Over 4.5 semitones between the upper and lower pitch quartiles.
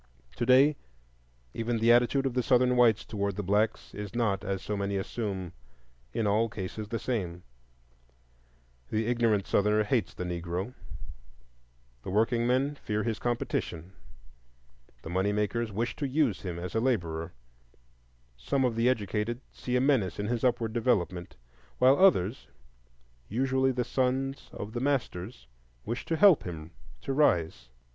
Yes: average, 5.0 semitones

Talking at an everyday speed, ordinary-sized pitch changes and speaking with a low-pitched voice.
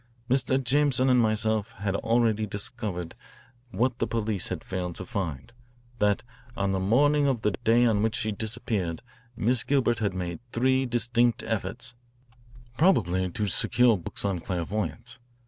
Yes: average, 145 wpm; average, 3.8 semitones; low, 110 Hz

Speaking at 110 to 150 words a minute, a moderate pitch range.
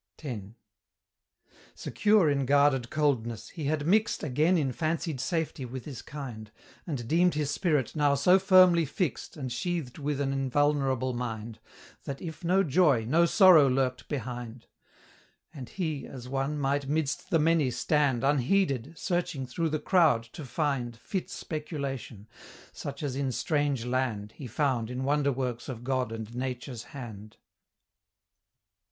Yes: average, 145 wpm; average, 3.9 semitones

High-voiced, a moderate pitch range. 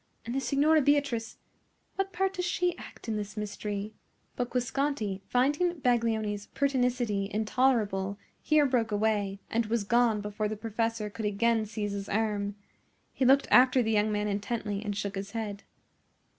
Yes: high, 225 Hz; average, 3.6 semitones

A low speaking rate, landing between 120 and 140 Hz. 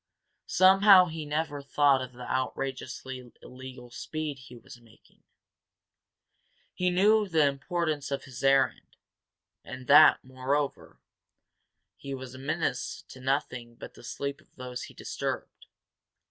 Yes: slow, 130 wpm; low, 135 Hz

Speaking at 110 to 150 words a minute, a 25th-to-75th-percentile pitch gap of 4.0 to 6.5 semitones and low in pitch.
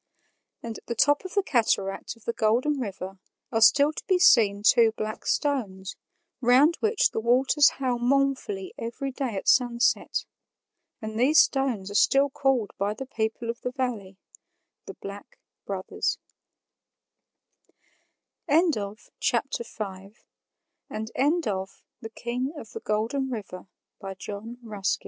No: slow, 135 wpm; average, 4.7 semitones; high, 235 Hz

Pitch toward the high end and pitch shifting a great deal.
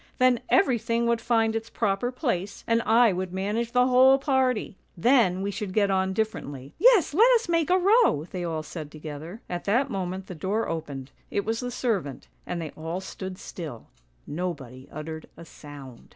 Yes: high, 200 Hz; wide, 6.6 semitones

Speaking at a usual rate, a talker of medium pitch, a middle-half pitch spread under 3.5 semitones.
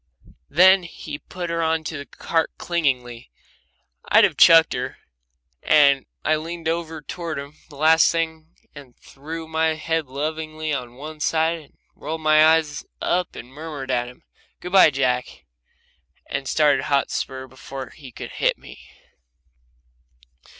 Yes: average, 145 wpm; medium, 155 Hz; average, 2.8 semitones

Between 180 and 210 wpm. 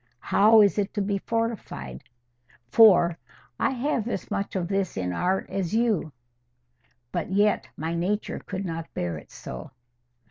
No: average, 150 wpm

